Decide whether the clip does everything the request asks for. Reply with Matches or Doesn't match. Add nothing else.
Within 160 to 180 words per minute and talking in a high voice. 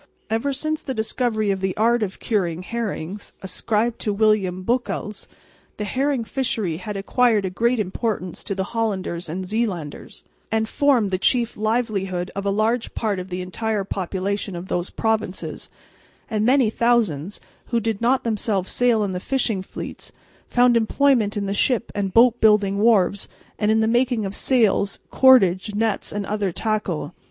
Matches